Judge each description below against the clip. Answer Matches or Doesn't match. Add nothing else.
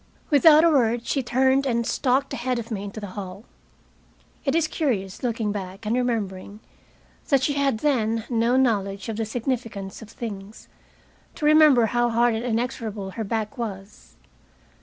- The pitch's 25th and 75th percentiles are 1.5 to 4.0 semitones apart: Matches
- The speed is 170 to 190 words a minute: Doesn't match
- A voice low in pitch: Doesn't match